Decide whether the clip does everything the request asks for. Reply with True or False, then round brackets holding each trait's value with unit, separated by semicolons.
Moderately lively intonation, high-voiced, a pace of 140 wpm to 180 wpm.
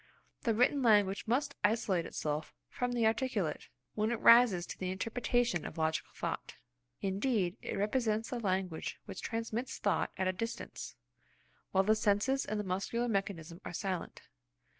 True (3.9 semitones; 210 Hz; 155 wpm)